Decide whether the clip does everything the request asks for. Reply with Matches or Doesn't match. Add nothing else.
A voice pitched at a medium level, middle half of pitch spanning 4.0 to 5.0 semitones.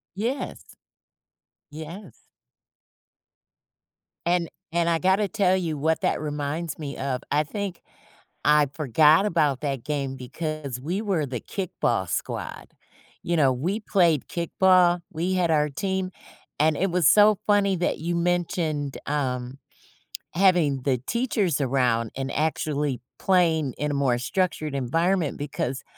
Matches